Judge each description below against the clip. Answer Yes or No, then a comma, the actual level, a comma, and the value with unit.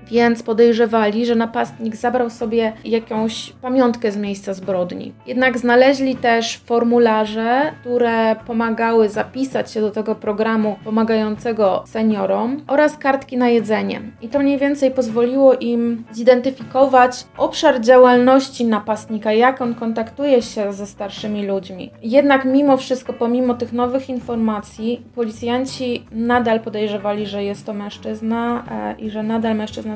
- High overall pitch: Yes, high, 235 Hz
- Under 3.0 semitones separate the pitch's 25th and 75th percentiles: Yes, narrow, 2.4 semitones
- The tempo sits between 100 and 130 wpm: Yes, average, 125 wpm